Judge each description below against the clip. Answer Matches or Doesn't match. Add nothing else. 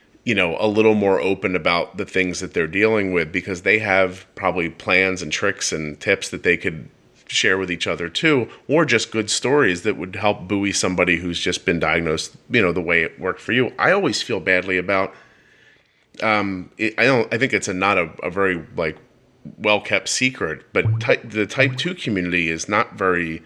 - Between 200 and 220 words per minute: Matches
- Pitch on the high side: Doesn't match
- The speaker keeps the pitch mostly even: Doesn't match